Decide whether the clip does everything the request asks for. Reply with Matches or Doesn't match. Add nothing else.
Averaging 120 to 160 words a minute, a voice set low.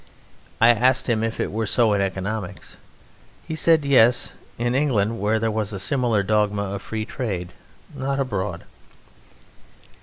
Matches